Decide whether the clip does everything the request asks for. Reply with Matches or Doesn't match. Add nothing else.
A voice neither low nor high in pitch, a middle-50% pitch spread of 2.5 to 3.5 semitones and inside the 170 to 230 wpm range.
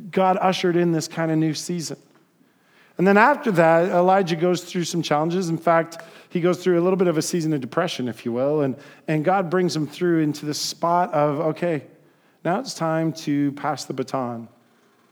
Matches